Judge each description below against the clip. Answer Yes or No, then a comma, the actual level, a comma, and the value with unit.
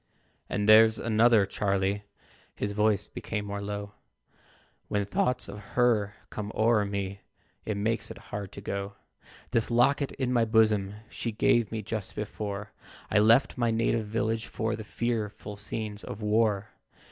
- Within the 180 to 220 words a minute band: No, average, 150 wpm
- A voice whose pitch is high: No, low, 105 Hz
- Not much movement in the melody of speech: Yes, narrow, 1.8 semitones